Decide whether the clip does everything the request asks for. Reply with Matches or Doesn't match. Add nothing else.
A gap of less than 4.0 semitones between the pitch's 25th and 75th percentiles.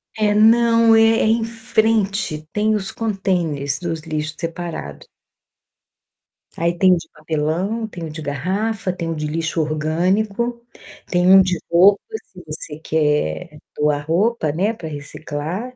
Doesn't match